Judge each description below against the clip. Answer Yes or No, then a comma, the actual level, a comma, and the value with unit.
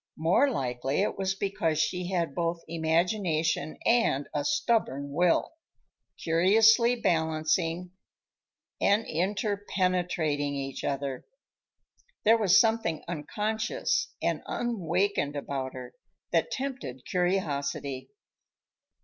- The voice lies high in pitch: No, medium, 170 Hz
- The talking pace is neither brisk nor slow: No, slow, 95 wpm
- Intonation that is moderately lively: No, wide, 5.7 semitones